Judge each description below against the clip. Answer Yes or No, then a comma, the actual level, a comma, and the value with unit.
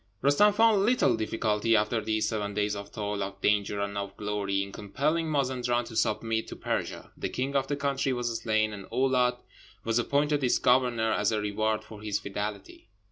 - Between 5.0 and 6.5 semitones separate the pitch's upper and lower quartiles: No, average, 4.0 semitones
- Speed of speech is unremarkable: Yes, average, 190 wpm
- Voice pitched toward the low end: Yes, low, 110 Hz